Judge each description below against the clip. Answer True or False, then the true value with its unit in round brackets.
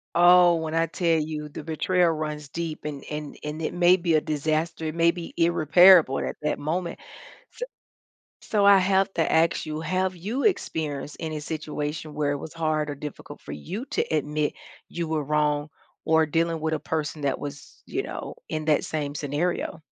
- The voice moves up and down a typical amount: False (2.1 semitones)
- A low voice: False (155 Hz)